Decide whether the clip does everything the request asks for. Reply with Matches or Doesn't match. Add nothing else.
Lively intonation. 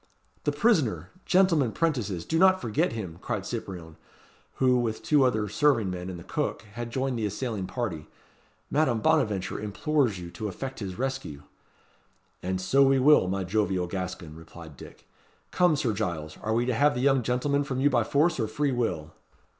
Matches